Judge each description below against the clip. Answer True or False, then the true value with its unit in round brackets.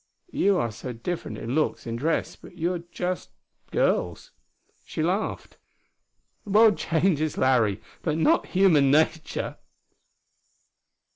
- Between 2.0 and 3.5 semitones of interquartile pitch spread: False (5.5 semitones)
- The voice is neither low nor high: True (160 Hz)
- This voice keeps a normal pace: False (120 wpm)